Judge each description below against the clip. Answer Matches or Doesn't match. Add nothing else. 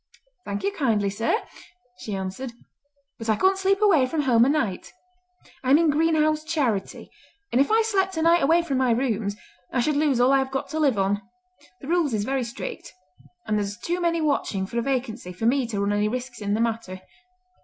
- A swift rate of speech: Matches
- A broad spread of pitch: Matches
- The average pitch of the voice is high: Matches